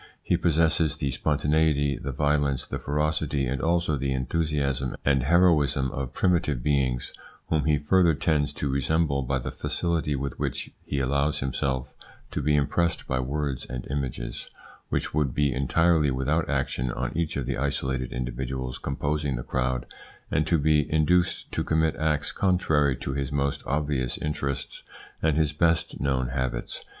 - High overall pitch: No, very low, 70 Hz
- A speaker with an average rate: Yes, average, 160 wpm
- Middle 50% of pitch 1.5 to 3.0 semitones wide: Yes, average, 2.7 semitones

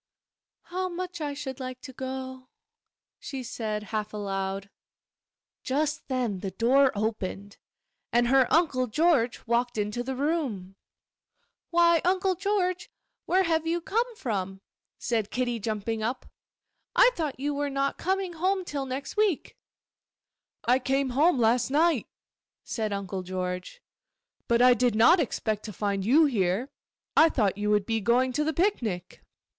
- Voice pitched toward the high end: Yes, very high, 255 Hz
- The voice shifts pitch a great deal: Yes, wide, 6.8 semitones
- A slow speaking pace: No, average, 145 wpm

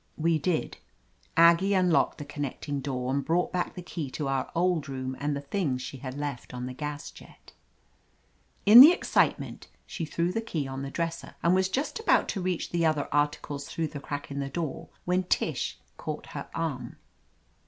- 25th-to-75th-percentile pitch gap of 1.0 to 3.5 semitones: No, average, 4.2 semitones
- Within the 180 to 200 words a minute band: Yes, average, 190 wpm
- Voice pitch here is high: No, medium, 150 Hz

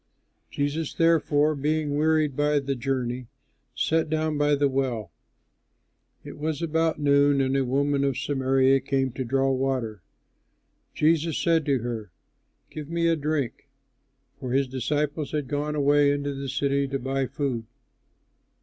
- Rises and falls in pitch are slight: Yes, narrow, 2.1 semitones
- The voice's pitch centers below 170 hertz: Yes, medium, 140 Hz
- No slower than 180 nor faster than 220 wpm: No, average, 145 wpm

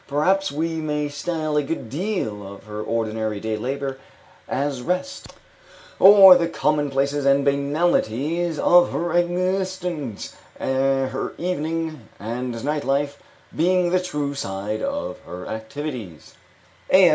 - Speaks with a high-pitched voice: No, medium, 145 Hz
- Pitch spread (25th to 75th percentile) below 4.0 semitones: No, average, 5.3 semitones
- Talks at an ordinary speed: No, slow, 120 wpm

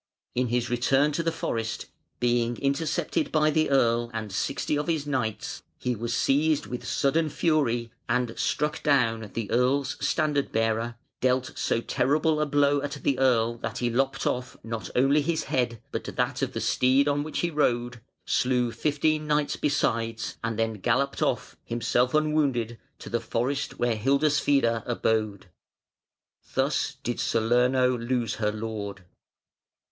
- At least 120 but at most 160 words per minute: Yes, average, 150 wpm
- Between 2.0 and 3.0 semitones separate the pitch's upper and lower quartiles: No, average, 3.8 semitones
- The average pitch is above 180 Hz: No, low, 125 Hz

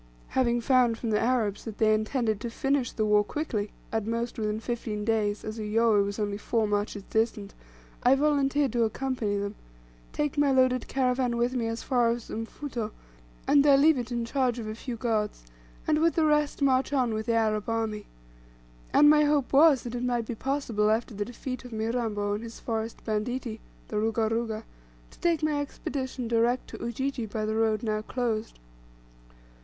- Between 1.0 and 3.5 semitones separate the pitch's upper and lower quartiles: Yes, average, 3.2 semitones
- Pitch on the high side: Yes, high, 230 Hz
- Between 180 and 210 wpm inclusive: Yes, average, 190 wpm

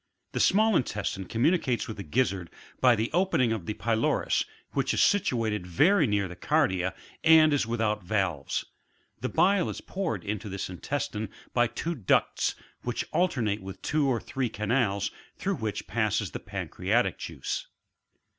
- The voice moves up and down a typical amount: No, wide, 6.6 semitones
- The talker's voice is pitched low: Yes, low, 115 Hz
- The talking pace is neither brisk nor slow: Yes, average, 155 wpm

